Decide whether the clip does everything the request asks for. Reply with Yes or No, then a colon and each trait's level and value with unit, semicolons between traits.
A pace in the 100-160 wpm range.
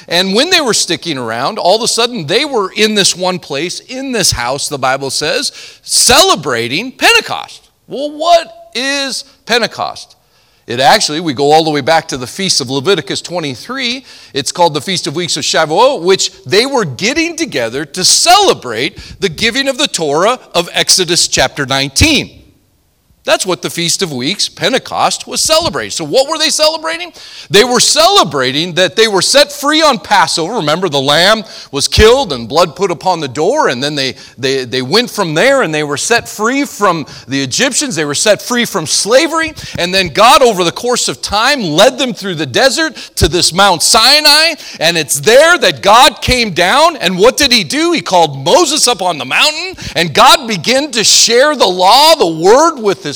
No: average, 190 wpm